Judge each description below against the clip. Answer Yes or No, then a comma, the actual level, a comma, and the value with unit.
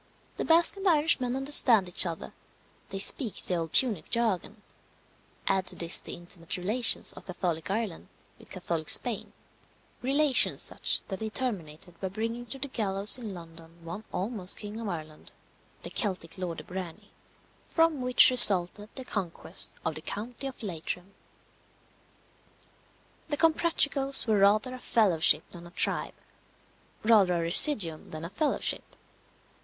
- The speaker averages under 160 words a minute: Yes, average, 150 wpm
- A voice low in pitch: No, high, 205 Hz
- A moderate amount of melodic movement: No, wide, 6.3 semitones